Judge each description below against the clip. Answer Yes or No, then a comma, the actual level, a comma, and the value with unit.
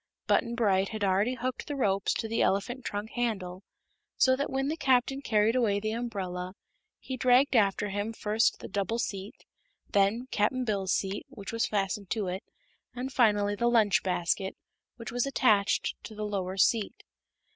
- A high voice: Yes, high, 215 Hz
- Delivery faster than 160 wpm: Yes, average, 170 wpm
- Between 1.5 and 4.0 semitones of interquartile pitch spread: Yes, average, 3.7 semitones